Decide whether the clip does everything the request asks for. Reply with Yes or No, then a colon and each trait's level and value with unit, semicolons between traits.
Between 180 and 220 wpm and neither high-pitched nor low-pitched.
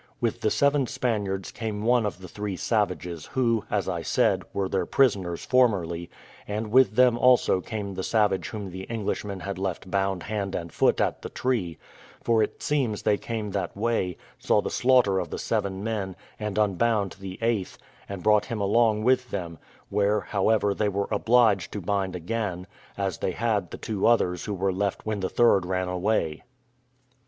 No: average, 185 wpm; low, 100 Hz